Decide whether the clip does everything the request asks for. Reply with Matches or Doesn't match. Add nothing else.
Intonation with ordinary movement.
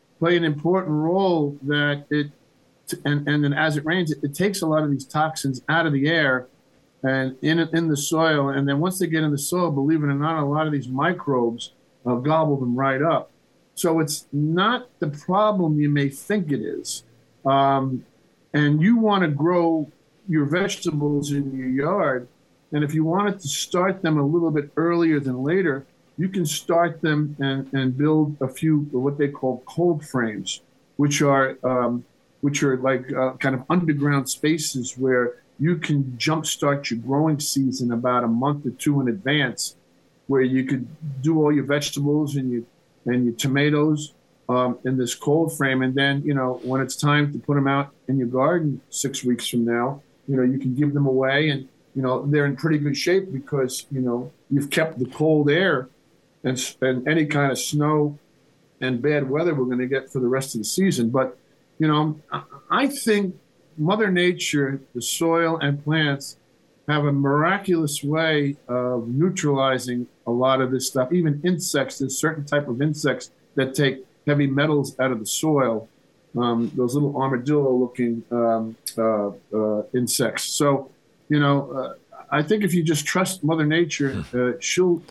Matches